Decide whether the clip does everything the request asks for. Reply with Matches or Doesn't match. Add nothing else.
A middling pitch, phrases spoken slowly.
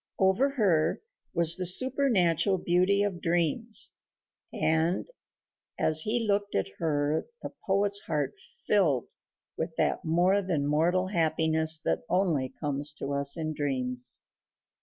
Matches